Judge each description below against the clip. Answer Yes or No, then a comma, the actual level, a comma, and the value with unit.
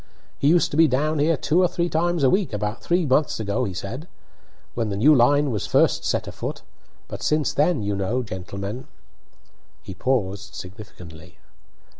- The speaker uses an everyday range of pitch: No, wide, 7.3 semitones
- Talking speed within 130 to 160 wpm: No, average, 180 wpm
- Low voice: Yes, low, 125 Hz